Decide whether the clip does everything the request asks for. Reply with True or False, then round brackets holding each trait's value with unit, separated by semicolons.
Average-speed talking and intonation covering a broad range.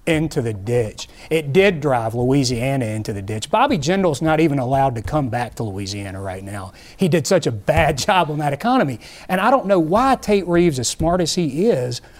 False (210 wpm; 7.4 semitones)